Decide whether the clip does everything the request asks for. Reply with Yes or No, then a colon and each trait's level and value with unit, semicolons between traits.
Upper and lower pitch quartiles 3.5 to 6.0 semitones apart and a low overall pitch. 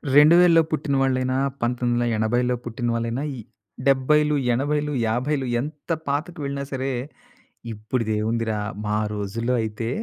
Yes: average, 3.8 semitones; low, 130 Hz